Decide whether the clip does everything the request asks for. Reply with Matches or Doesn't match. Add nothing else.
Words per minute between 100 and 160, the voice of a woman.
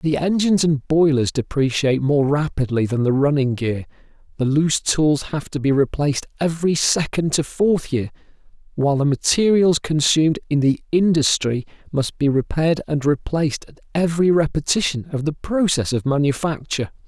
Doesn't match